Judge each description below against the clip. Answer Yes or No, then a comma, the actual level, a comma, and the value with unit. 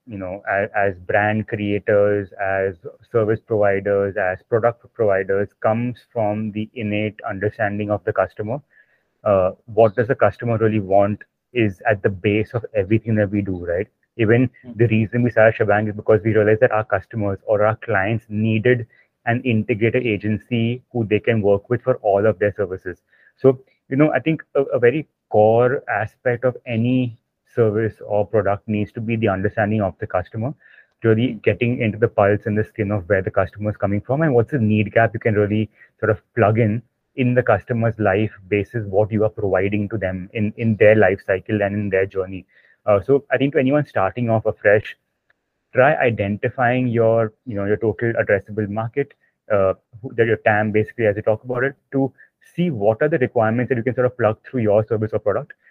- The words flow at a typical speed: Yes, average, 195 wpm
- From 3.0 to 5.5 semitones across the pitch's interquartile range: No, narrow, 2.4 semitones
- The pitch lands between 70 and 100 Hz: No, low, 110 Hz